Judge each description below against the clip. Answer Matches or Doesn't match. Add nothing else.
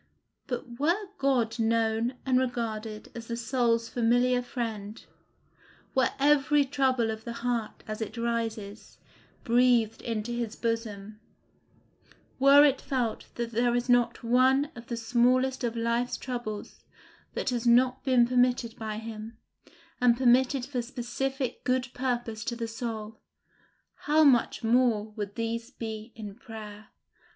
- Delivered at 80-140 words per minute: Matches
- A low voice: Doesn't match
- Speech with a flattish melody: Matches